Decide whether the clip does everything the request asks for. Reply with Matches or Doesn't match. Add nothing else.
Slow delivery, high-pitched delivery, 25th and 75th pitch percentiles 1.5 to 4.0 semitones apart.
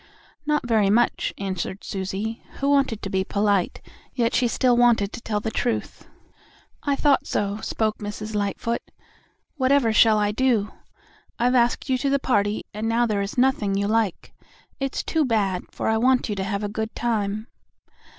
Doesn't match